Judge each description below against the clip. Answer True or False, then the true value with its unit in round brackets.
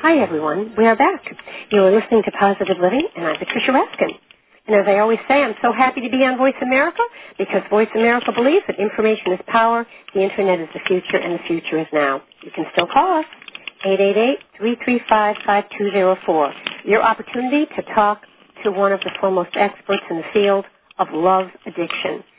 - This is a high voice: True (205 Hz)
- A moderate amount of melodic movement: True (3.9 semitones)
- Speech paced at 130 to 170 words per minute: False (180 wpm)